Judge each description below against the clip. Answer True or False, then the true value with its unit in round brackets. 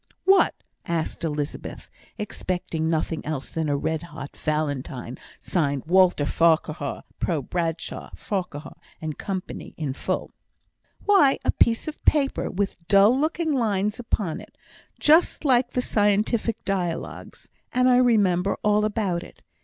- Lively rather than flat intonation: True (6.4 semitones)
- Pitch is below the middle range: False (185 Hz)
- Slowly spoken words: True (130 wpm)